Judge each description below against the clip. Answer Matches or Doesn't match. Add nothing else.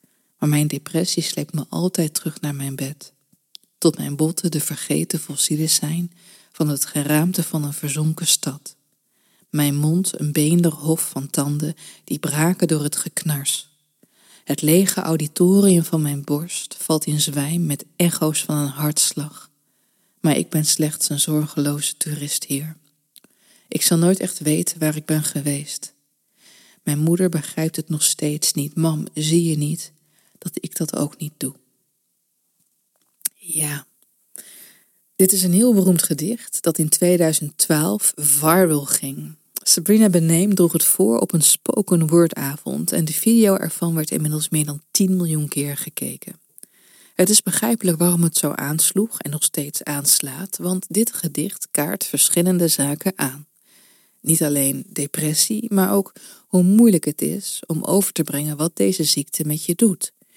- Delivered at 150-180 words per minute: Matches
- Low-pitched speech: Doesn't match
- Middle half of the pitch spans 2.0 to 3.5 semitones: Matches